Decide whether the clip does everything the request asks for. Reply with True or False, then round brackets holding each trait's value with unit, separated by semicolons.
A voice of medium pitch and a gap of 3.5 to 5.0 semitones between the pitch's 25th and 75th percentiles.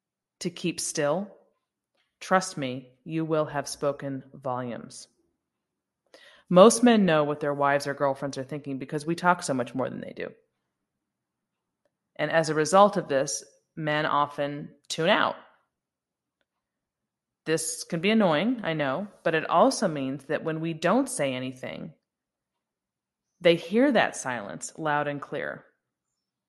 True (155 Hz; 4.1 semitones)